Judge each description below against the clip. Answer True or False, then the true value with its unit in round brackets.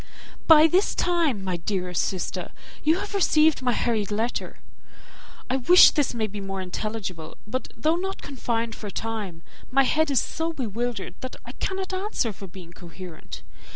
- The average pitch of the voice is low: False (230 Hz)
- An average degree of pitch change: False (8.3 semitones)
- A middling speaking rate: True (160 wpm)